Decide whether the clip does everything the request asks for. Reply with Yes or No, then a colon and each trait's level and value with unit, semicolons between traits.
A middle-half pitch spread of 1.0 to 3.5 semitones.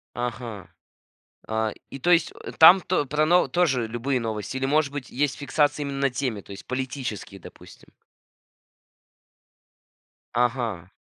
No: average, 4.1 semitones